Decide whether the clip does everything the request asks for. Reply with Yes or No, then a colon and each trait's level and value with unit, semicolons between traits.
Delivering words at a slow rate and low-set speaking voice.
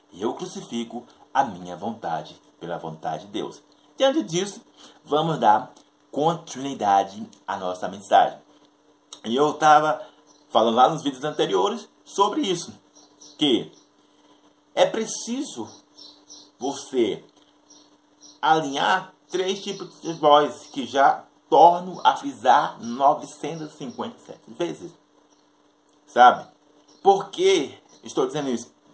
No: slow, 100 wpm; medium, 165 Hz